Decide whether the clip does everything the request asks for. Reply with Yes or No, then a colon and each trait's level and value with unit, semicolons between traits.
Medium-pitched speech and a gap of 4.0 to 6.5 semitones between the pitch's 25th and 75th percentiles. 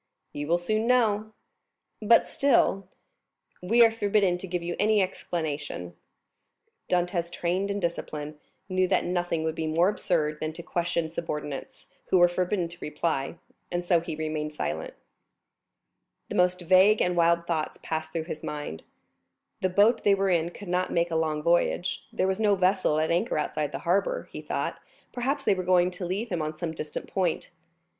No: medium, 175 Hz; average, 3.1 semitones